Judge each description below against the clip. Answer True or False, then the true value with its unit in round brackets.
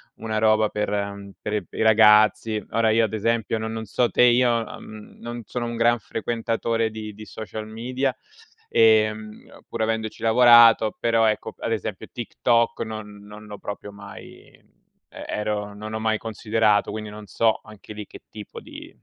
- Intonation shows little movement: True (1.3 semitones)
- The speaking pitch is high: False (110 Hz)